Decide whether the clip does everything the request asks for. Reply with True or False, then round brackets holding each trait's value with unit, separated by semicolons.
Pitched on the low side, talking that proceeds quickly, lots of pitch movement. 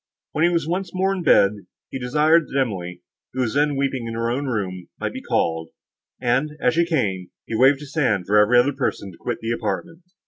True (130 Hz; 220 wpm; 6.3 semitones)